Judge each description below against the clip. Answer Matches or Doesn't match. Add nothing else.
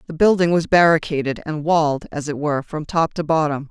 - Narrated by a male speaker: Doesn't match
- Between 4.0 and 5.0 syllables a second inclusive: Doesn't match